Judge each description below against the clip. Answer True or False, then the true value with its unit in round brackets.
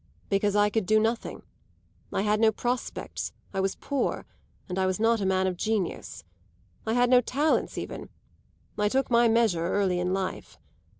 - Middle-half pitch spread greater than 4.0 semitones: False (3.5 semitones)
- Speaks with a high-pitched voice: True (210 Hz)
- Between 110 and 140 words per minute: False (175 wpm)